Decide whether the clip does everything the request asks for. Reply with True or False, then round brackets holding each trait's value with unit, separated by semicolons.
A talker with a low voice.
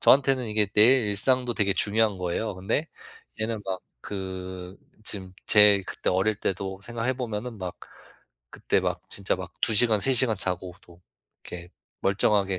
True (100 Hz)